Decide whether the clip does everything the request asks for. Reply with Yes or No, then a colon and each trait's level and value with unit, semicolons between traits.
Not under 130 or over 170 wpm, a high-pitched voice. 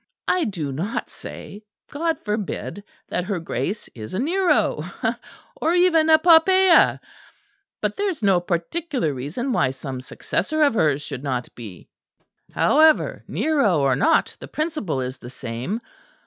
Yes: average, 145 wpm; high, 205 Hz